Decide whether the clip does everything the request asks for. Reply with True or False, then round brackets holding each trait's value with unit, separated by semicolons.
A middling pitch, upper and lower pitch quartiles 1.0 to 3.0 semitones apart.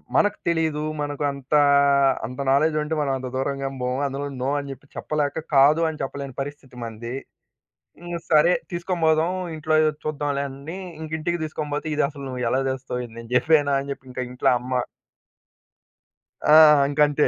True (145 Hz; 2.5 semitones)